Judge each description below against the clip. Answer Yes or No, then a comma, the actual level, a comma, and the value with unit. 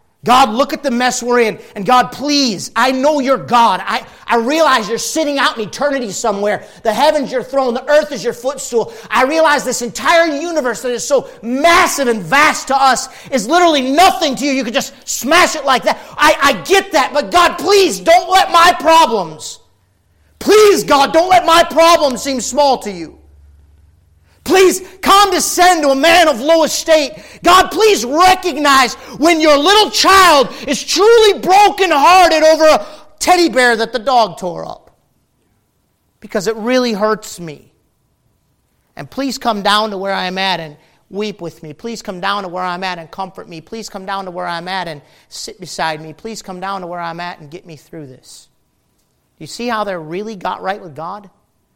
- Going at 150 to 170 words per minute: No, average, 190 wpm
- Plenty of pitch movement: Yes, wide, 7.3 semitones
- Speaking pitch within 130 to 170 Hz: No, very high, 260 Hz